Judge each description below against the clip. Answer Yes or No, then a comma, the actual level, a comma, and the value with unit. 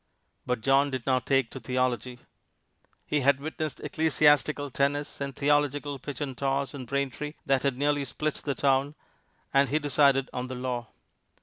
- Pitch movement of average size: No, narrow, 2.0 semitones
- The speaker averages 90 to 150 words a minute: No, average, 165 wpm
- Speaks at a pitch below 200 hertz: Yes, medium, 140 Hz